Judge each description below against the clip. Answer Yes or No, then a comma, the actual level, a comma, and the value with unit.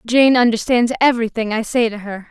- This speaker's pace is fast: No, average, 185 wpm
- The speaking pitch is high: Yes, high, 230 Hz